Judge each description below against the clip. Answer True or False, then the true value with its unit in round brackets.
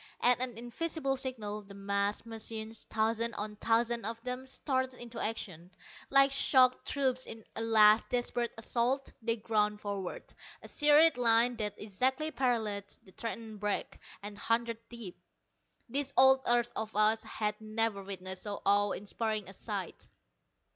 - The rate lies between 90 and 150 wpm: True (145 wpm)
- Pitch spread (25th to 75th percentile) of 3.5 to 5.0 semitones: False (3.0 semitones)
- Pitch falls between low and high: False (225 Hz)